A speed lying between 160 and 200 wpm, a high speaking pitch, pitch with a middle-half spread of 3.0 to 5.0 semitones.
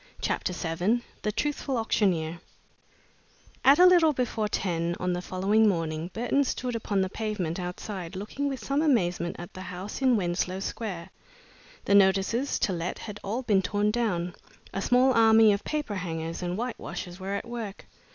Yes: average, 170 wpm; high, 200 Hz; average, 4.7 semitones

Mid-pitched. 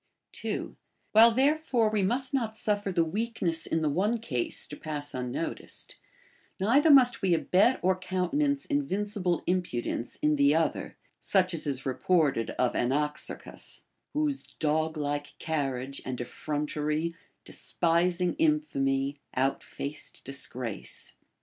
Yes: medium, 170 Hz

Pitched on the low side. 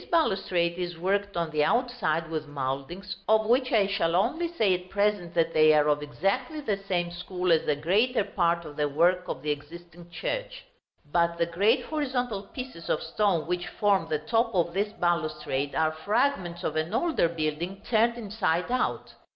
No: medium, 180 Hz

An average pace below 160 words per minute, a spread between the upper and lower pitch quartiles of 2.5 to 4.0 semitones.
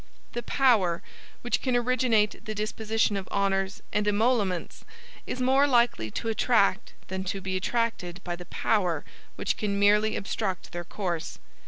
Yes: average, 150 wpm; average, 3.7 semitones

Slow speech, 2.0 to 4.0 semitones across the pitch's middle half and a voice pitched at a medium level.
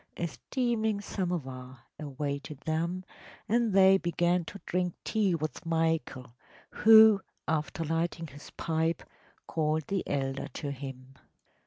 No: slow, 120 wpm; average, 4.7 semitones; medium, 165 Hz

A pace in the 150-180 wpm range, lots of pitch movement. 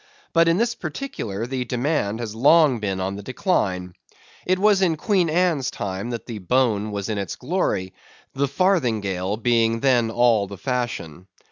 Yes: average, 165 wpm; wide, 7.7 semitones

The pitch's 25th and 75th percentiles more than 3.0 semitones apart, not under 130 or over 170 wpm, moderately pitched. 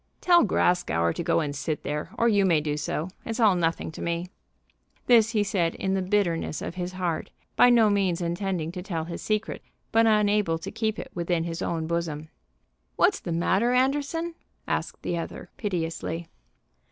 No: average, 4.3 semitones; average, 180 wpm; medium, 180 Hz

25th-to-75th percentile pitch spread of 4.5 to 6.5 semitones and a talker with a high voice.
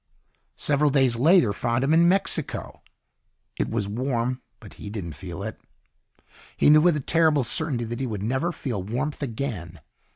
No: wide, 5.5 semitones; low, 130 Hz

